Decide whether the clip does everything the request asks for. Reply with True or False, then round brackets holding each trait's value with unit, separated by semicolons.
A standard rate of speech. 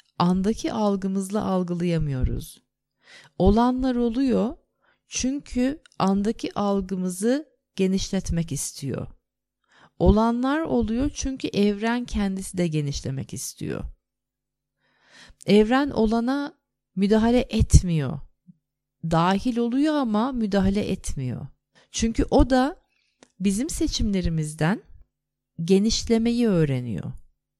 False (75 wpm)